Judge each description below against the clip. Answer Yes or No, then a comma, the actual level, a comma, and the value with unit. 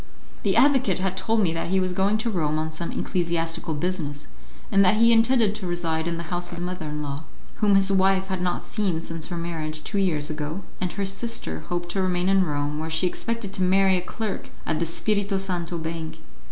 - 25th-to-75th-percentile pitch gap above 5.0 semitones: No, average, 3.1 semitones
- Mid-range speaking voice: Yes, medium, 180 Hz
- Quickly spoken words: Yes, fast, 220 wpm